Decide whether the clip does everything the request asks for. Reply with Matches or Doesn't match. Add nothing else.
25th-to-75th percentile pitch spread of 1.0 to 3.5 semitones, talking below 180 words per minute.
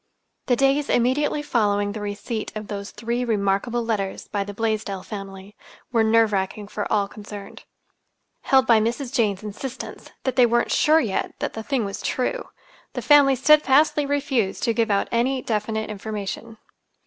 Doesn't match